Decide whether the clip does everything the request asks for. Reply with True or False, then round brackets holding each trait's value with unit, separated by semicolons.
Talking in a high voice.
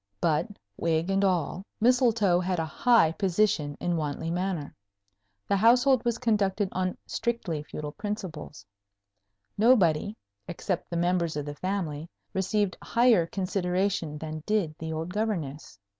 False (180 Hz)